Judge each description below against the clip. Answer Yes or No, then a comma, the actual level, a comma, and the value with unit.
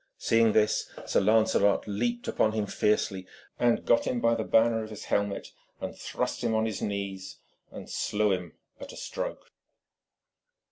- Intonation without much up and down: Yes, narrow, 2.1 semitones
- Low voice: Yes, low, 110 Hz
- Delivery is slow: No, average, 160 wpm